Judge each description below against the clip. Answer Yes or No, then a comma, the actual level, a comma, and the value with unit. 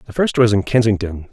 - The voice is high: No, low, 110 Hz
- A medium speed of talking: No, fast, 225 wpm